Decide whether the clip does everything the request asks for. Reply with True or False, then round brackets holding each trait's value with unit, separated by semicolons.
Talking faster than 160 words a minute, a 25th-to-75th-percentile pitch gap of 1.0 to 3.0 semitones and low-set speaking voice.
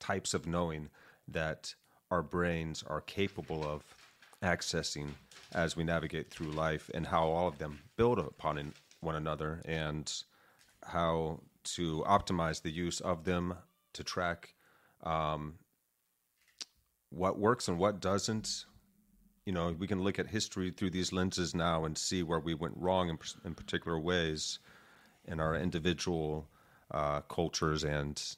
False (140 wpm; 2.7 semitones; 85 Hz)